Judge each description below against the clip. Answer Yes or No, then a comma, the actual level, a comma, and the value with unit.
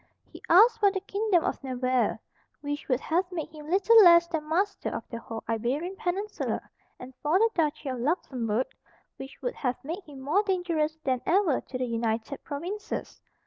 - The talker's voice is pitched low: No, very high, 315 Hz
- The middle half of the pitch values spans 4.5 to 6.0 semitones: No, wide, 6.6 semitones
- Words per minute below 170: No, average, 180 wpm